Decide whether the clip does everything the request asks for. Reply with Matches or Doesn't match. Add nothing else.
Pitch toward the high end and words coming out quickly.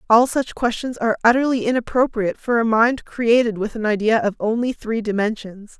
Doesn't match